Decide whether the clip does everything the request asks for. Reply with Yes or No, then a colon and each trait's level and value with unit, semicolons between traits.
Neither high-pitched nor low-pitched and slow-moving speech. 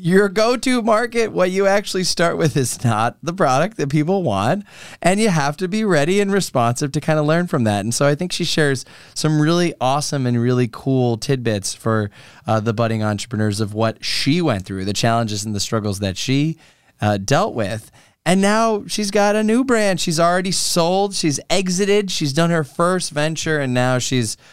No: medium, 150 Hz; fast, 205 wpm